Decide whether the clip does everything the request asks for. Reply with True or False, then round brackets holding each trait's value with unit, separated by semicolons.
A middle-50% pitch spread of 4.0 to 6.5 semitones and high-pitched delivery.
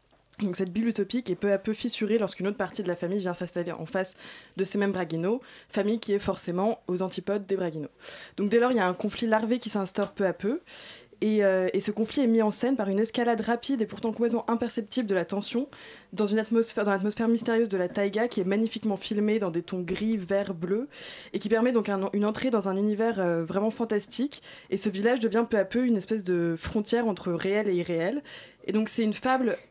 False (3.0 semitones; 210 Hz)